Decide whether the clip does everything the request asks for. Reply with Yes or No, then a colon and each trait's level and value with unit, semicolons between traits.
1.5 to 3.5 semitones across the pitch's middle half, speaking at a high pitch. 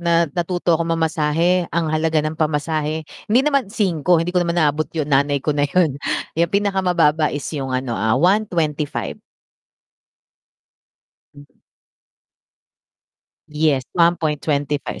No: average, 2.8 semitones; medium, 160 Hz